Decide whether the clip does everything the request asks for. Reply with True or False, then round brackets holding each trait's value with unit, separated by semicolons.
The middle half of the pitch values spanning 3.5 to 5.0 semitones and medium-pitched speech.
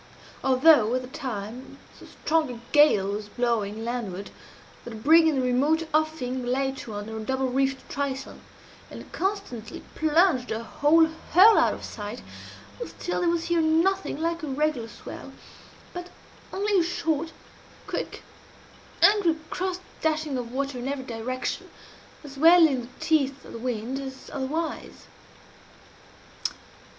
False (4.7 semitones; 270 Hz)